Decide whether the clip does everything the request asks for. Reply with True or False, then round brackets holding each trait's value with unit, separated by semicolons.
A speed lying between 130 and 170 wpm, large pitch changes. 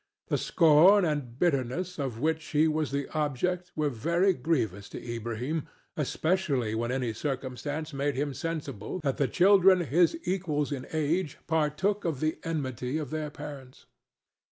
False (150 wpm; 4.1 semitones)